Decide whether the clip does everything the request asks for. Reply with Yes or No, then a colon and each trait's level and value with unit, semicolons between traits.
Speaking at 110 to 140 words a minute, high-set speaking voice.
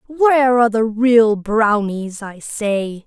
Yes: slow, 135 wpm; high, 225 Hz